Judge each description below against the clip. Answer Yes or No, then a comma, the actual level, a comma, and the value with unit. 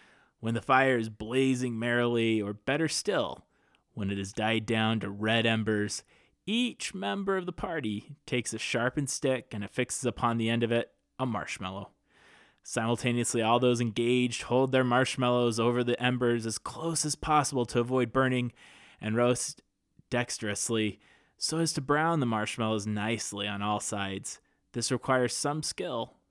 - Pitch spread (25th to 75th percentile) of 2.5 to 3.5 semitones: Yes, average, 2.9 semitones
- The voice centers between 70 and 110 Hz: No, low, 120 Hz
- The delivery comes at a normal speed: Yes, average, 155 wpm